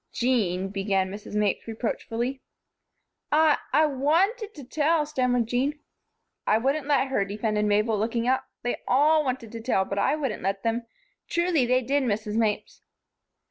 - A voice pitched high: Yes, high, 245 Hz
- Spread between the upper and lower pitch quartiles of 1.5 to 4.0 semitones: No, average, 5.3 semitones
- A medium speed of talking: Yes, average, 155 wpm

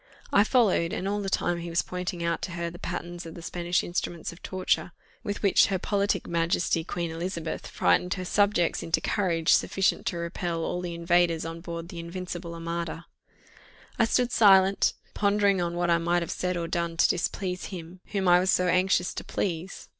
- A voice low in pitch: No, medium, 175 Hz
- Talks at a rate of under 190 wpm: No, average, 195 wpm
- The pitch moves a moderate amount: No, narrow, 1.9 semitones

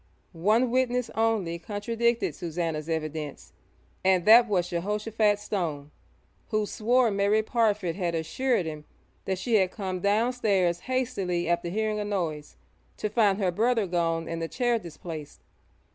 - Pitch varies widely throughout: No, average, 4.7 semitones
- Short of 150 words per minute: Yes, average, 140 wpm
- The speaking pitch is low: No, high, 200 Hz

